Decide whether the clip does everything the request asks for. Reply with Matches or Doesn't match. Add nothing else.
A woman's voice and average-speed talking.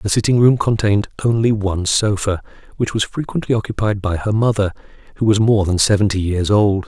Doesn't match